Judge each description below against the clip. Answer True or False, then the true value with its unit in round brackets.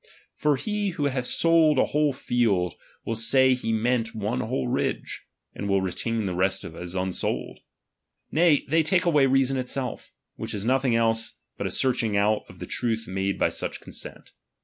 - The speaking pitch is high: False (120 Hz)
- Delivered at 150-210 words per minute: True (180 wpm)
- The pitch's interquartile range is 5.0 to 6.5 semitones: True (5.3 semitones)